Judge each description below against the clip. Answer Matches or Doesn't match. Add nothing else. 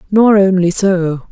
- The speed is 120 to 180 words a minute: Matches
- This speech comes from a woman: Matches